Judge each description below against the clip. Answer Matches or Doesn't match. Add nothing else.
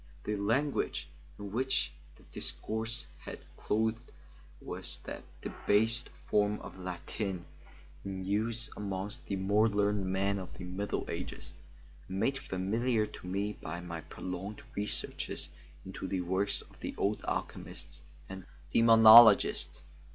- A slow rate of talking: Matches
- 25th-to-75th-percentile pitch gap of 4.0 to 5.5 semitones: Doesn't match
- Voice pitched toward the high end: Doesn't match